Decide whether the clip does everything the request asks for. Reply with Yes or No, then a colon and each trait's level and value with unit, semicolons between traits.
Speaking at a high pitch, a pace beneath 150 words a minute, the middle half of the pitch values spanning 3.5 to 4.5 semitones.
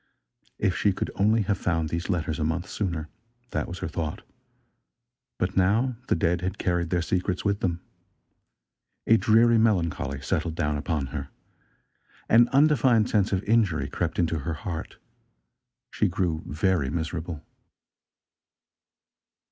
No: very low, 90 Hz; average, 140 wpm; average, 4.2 semitones